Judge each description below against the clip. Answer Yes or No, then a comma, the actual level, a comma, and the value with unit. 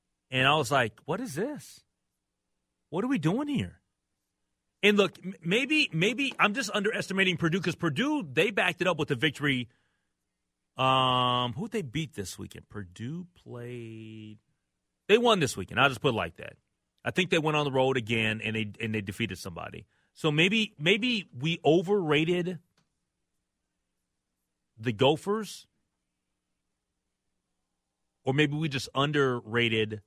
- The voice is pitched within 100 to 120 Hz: No, low, 135 Hz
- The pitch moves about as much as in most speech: No, wide, 8.6 semitones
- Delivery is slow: No, average, 150 wpm